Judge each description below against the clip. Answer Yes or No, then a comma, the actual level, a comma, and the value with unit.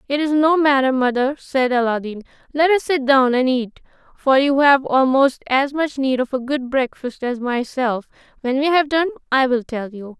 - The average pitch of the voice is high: Yes, very high, 265 Hz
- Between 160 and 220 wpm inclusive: Yes, average, 200 wpm